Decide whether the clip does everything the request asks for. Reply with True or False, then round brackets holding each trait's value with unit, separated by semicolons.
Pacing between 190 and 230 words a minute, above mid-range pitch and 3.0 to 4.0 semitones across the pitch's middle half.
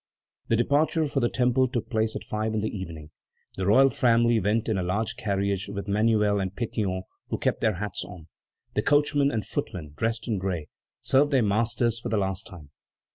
False (195 wpm; 110 Hz; 3.5 semitones)